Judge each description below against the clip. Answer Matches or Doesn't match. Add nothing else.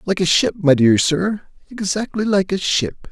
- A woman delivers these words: Doesn't match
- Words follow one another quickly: Doesn't match